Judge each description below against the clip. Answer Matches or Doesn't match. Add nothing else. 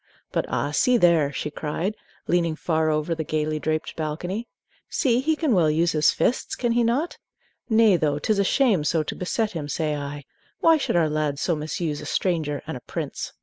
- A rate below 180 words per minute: Doesn't match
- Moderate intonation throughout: Doesn't match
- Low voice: Doesn't match